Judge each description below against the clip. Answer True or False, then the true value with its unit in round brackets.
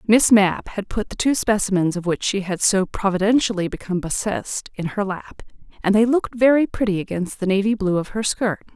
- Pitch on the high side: True (200 Hz)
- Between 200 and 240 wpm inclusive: True (205 wpm)